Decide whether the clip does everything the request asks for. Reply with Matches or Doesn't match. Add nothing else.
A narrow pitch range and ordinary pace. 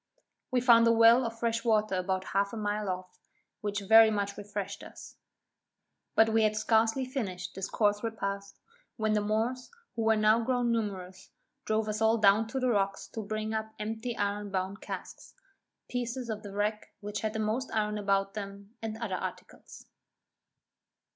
Matches